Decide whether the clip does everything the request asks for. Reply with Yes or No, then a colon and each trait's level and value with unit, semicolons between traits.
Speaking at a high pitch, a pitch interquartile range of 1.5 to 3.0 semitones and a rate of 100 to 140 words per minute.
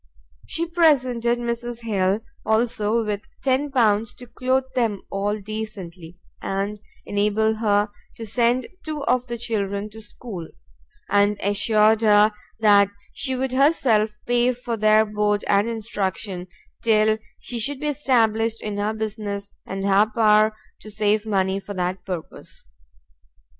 Yes: high, 215 Hz; narrow, 2.6 semitones; slow, 135 wpm